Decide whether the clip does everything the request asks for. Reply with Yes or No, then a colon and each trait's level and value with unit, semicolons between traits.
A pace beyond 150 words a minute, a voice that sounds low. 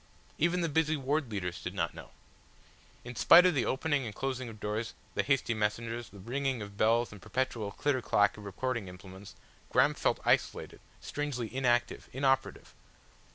Yes: average, 170 wpm; low, 120 Hz